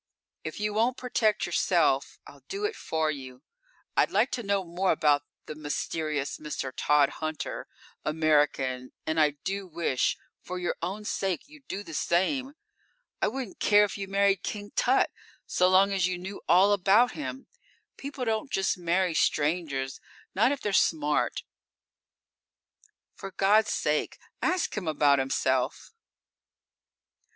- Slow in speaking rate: No, average, 145 wpm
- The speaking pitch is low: No, medium, 185 Hz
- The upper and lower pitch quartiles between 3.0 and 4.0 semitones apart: No, wide, 5.4 semitones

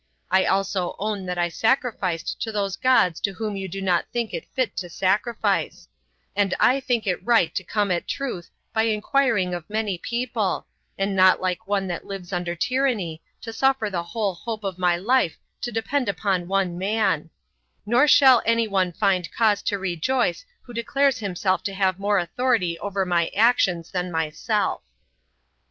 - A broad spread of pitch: No, average, 4.1 semitones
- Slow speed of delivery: No, average, 175 wpm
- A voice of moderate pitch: No, high, 195 Hz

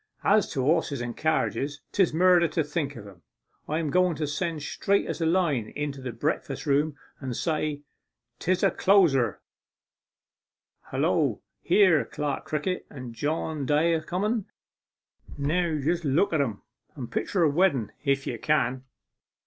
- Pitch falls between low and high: Yes, medium, 150 Hz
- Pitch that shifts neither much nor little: Yes, average, 3.7 semitones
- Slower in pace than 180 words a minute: Yes, average, 155 wpm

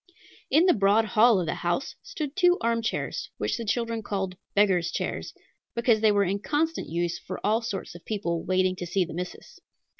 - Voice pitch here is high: Yes, high, 205 Hz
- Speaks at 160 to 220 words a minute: Yes, average, 190 wpm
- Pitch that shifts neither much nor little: Yes, average, 4.3 semitones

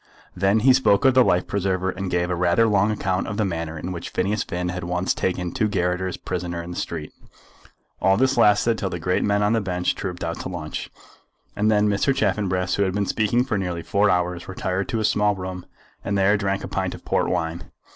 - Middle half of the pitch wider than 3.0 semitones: No, average, 2.7 semitones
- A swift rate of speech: Yes, fast, 225 wpm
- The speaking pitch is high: No, very low, 95 Hz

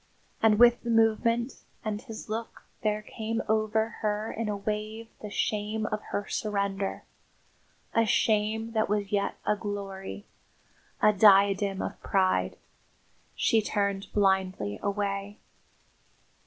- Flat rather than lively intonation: Yes, narrow, 1.7 semitones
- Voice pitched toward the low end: No, high, 210 Hz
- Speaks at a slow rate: Yes, slow, 125 wpm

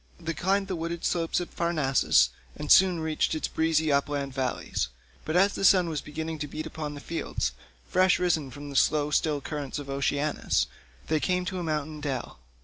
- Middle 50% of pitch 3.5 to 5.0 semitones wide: No, average, 2.9 semitones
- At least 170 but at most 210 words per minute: Yes, average, 190 wpm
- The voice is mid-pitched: Yes, medium, 155 Hz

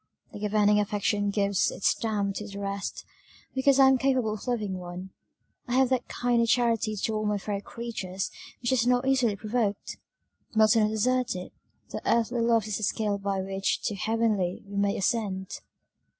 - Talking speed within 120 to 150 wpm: No, average, 180 wpm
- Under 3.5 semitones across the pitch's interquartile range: Yes, average, 2.9 semitones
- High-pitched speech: Yes, high, 215 Hz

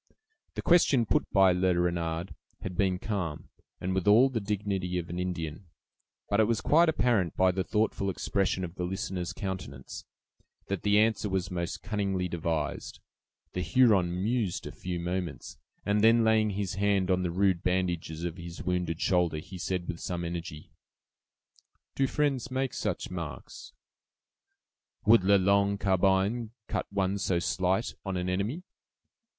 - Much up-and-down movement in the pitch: No, average, 2.7 semitones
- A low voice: Yes, very low, 95 Hz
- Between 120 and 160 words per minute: Yes, average, 155 wpm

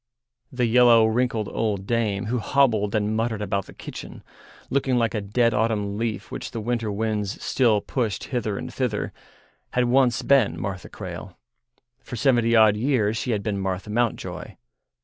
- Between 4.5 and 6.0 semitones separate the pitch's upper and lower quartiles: No, average, 2.7 semitones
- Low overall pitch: Yes, low, 110 Hz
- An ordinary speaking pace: Yes, average, 165 wpm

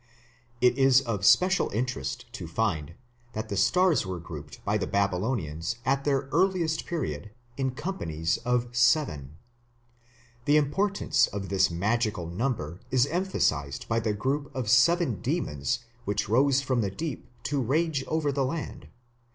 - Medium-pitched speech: No, low, 120 Hz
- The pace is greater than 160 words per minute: No, average, 150 wpm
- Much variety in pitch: Yes, wide, 6.8 semitones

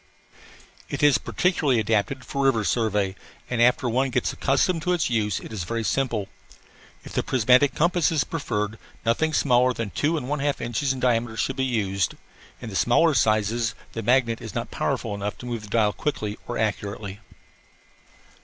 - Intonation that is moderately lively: Yes, average, 4.0 semitones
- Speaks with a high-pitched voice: No, low, 120 Hz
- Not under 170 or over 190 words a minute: Yes, average, 180 wpm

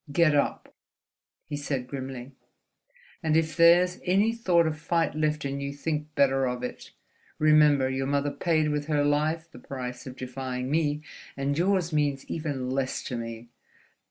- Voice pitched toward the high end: No, medium, 145 Hz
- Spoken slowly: No, average, 160 wpm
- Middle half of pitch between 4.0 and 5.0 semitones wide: No, average, 3.0 semitones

